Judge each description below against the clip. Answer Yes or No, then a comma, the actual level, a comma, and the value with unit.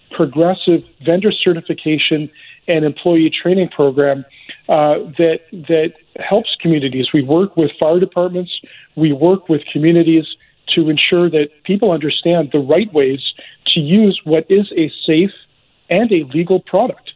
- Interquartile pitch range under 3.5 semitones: Yes, average, 2.8 semitones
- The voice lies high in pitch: No, medium, 165 Hz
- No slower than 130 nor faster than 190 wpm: Yes, slow, 135 wpm